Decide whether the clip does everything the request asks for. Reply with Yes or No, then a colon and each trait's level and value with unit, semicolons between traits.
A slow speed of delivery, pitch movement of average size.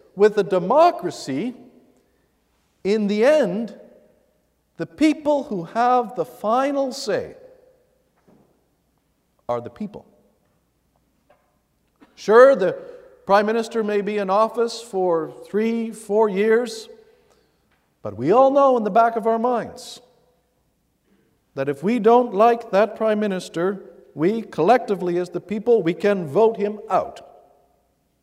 Yes: slow, 120 wpm; average, 3.8 semitones